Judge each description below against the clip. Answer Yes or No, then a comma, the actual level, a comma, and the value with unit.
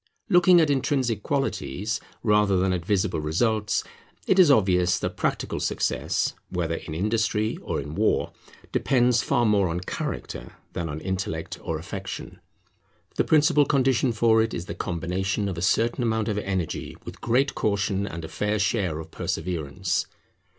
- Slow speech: No, average, 155 wpm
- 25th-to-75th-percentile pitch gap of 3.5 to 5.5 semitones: Yes, average, 4.7 semitones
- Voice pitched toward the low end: Yes, low, 105 Hz